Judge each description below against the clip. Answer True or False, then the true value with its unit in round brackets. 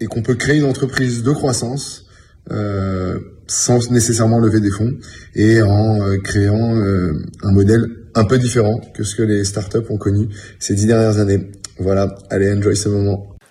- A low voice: True (105 Hz)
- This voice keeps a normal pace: True (180 wpm)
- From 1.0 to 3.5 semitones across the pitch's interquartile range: True (2.6 semitones)